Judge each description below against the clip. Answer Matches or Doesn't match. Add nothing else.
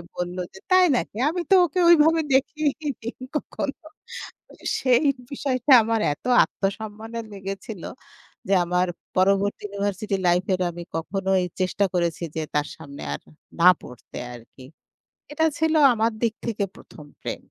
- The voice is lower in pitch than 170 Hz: Doesn't match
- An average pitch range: Doesn't match